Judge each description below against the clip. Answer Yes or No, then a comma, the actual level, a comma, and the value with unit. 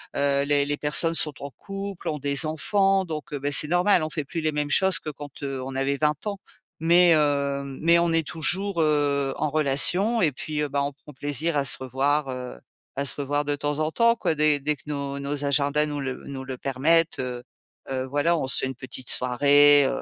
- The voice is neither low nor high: Yes, medium, 145 Hz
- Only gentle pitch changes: Yes, narrow, 2.3 semitones